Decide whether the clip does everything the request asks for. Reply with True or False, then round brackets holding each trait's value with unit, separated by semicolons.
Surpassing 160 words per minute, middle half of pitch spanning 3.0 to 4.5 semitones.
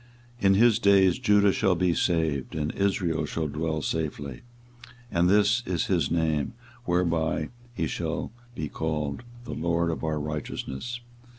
False (140 wpm; 3.9 semitones)